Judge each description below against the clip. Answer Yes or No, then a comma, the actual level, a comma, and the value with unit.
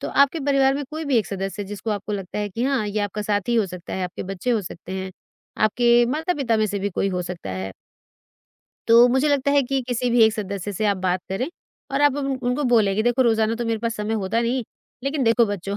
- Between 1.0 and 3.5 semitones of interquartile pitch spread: No, average, 4.2 semitones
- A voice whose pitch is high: Yes, high, 220 Hz